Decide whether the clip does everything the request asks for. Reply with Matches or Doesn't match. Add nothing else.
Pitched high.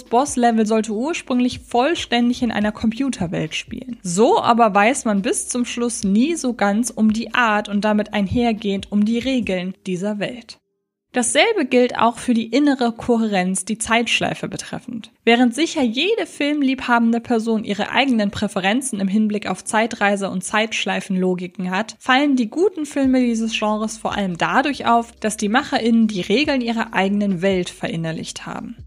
Matches